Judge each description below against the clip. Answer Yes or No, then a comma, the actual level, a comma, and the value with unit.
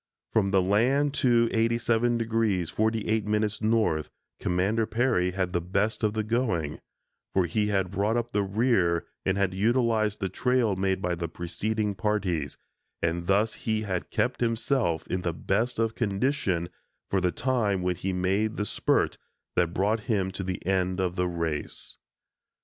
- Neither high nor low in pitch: No, low, 100 Hz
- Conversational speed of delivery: Yes, average, 160 wpm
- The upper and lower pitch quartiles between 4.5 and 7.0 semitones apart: No, average, 3.7 semitones